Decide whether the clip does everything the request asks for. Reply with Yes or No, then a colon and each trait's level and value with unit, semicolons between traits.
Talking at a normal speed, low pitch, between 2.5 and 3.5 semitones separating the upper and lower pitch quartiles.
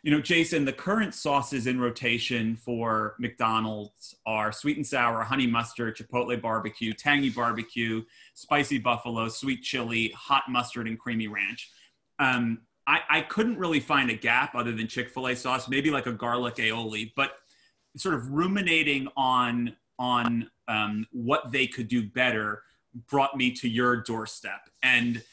Yes: average, 150 wpm; low, 120 Hz; average, 2.9 semitones